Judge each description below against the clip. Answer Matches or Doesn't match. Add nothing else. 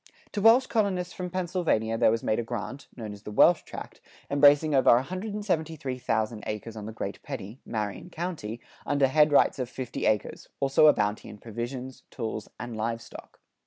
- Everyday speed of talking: Matches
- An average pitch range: Doesn't match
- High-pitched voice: Doesn't match